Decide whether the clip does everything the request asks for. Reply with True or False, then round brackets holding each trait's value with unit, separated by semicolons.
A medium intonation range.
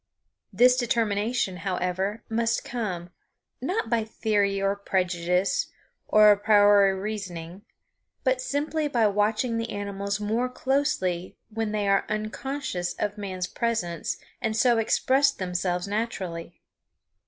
True (3.5 semitones)